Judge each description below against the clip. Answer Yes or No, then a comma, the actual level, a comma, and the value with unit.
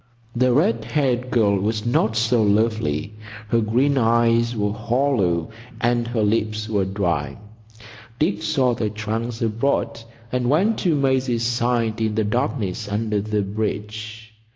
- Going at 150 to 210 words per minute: No, average, 140 wpm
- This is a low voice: Yes, low, 115 Hz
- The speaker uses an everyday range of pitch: No, narrow, 2.3 semitones